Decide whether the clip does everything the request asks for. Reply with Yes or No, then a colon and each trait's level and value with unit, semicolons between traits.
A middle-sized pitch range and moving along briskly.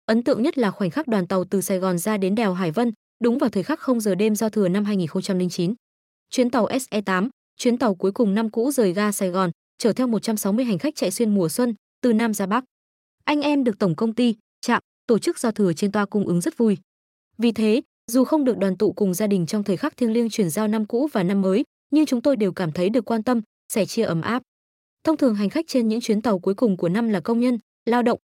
Yes: average, 3.8 semitones; fast, 260 wpm